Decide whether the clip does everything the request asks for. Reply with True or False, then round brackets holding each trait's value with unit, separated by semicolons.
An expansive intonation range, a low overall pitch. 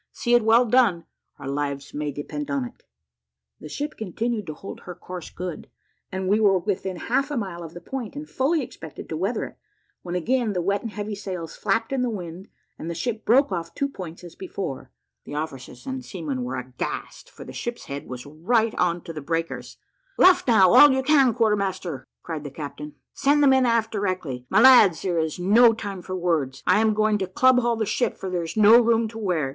False (6.0 semitones; 195 Hz)